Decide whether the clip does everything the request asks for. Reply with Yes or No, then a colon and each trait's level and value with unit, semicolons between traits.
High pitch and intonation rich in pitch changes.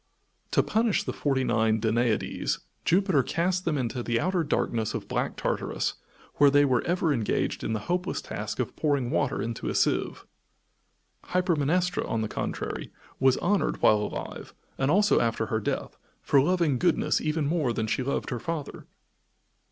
No: medium, 140 Hz; wide, 6.8 semitones